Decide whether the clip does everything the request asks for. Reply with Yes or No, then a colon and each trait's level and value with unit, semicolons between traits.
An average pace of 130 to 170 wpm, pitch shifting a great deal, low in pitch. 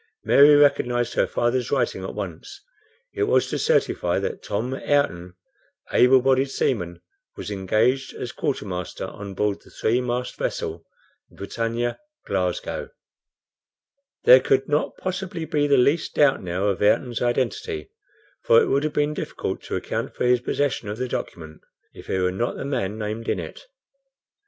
Yes: average, 160 wpm; wide, 5.7 semitones; low, 125 Hz